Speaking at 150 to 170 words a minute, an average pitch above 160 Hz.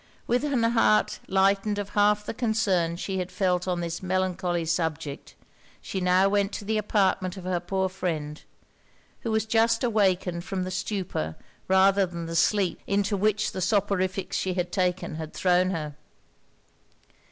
Yes: average, 160 wpm; high, 190 Hz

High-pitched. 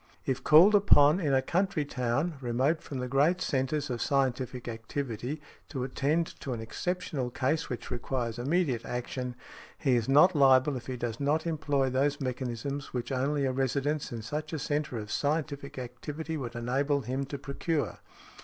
No: low, 135 Hz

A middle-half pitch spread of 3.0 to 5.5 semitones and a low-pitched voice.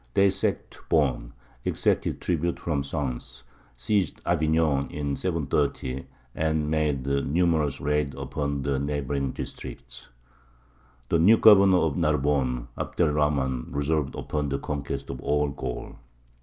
No: narrow, 2.4 semitones; very low, 75 Hz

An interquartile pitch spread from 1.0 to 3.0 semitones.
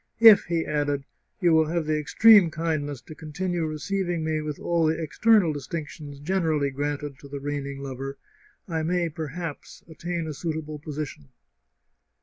Yes: average, 2.7 semitones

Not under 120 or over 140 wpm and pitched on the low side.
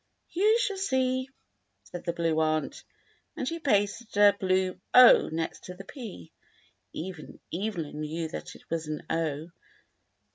No: slow, 135 wpm; medium, 185 Hz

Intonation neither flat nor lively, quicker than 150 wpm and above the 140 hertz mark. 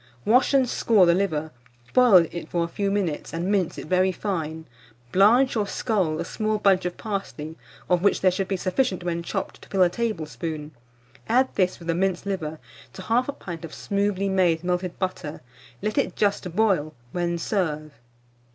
Yes: average, 3.3 semitones; average, 180 wpm; medium, 185 Hz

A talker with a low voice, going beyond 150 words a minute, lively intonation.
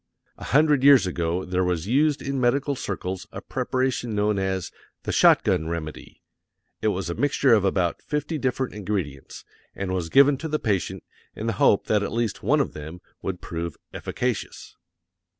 Yes: low, 105 Hz; average, 175 wpm; wide, 6.6 semitones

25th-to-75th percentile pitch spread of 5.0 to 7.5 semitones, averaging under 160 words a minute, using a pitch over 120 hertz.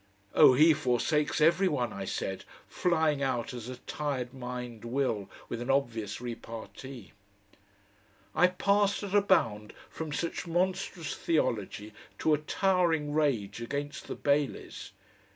Yes: wide, 5.5 semitones; slow, 135 wpm; medium, 140 Hz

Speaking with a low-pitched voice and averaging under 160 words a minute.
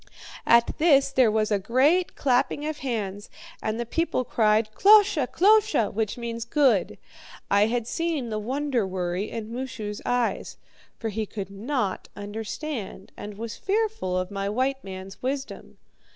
No: high, 230 Hz; average, 150 wpm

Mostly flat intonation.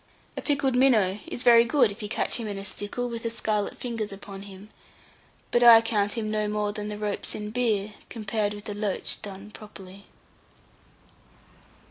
Yes: narrow, 2.2 semitones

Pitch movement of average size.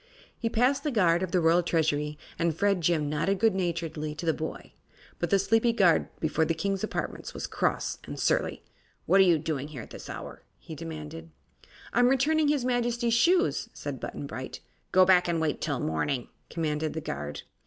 No: wide, 5.9 semitones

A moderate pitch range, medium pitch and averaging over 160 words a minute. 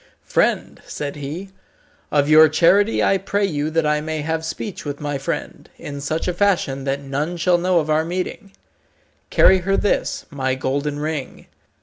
Yes: average, 3.8 semitones; medium, 155 Hz; average, 175 wpm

